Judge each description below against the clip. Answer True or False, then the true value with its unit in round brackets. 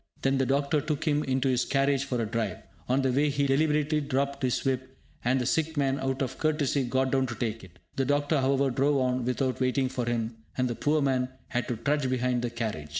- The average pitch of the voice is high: False (130 Hz)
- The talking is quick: True (230 wpm)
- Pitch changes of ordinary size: False (2.1 semitones)